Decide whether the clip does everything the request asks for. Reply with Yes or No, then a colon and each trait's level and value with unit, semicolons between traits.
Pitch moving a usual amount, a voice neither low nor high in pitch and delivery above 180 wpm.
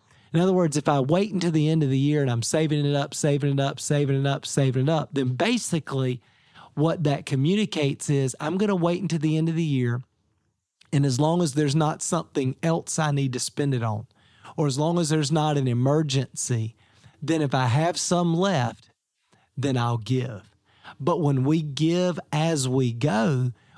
Yes: average, 3.9 semitones; medium, 145 Hz; average, 200 wpm